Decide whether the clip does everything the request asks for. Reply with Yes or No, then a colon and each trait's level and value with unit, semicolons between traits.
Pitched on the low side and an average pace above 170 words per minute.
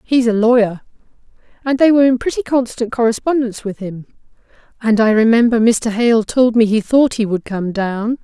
No: high, 230 Hz; average, 180 wpm